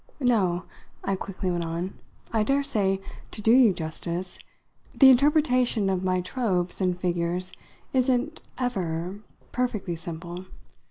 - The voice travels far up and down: Yes, wide, 5.8 semitones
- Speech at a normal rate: No, slow, 120 wpm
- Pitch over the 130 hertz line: Yes, high, 190 Hz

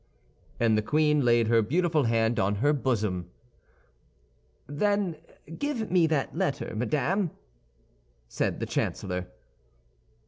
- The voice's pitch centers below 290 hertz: Yes, medium, 140 Hz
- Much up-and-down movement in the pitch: Yes, wide, 6.9 semitones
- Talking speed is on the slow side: Yes, slow, 110 wpm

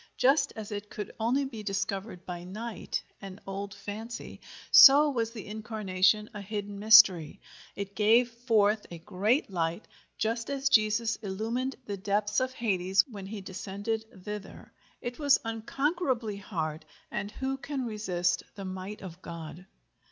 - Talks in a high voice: Yes, high, 210 Hz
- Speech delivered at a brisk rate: No, average, 140 wpm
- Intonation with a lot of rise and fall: No, average, 3.2 semitones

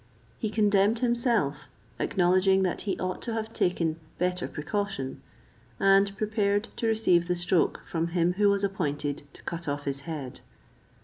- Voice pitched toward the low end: No, high, 190 Hz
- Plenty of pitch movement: No, average, 3.7 semitones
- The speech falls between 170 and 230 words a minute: No, average, 150 wpm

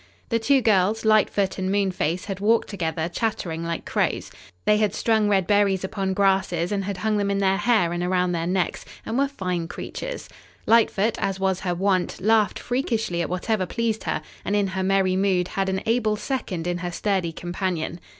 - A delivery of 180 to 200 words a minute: Yes, average, 190 wpm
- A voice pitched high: Yes, high, 195 Hz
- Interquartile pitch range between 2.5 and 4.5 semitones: Yes, average, 3.0 semitones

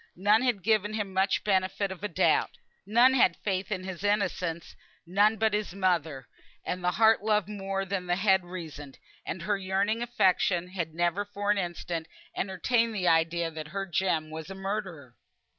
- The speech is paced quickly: No, average, 180 wpm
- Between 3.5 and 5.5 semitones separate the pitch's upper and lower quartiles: No, average, 3.1 semitones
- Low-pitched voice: No, high, 190 Hz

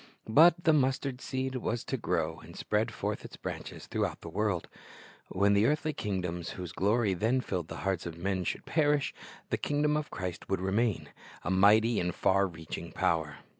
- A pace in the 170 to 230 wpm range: Yes, average, 180 wpm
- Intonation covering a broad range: Yes, wide, 6.5 semitones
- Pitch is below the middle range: Yes, low, 100 Hz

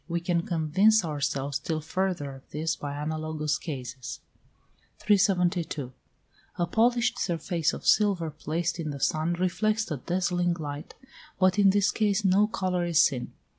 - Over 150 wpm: No, average, 145 wpm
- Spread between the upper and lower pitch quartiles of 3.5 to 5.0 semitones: Yes, average, 3.9 semitones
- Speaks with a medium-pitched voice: Yes, medium, 170 Hz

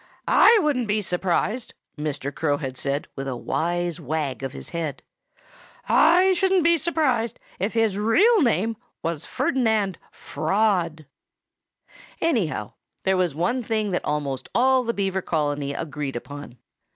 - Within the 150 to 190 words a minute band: No, average, 140 wpm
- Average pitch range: No, wide, 7.9 semitones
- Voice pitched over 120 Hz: Yes, medium, 185 Hz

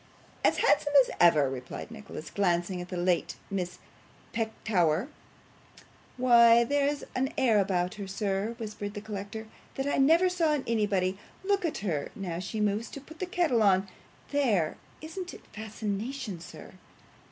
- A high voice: Yes, high, 210 Hz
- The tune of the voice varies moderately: No, wide, 5.9 semitones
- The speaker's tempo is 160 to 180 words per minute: No, average, 150 wpm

